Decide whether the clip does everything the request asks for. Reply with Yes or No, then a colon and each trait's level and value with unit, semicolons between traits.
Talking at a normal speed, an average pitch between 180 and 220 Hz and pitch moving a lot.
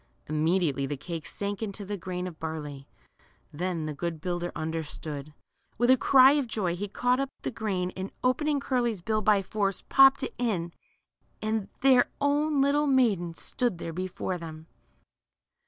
Yes: average, 170 wpm; high, 190 Hz; wide, 6.8 semitones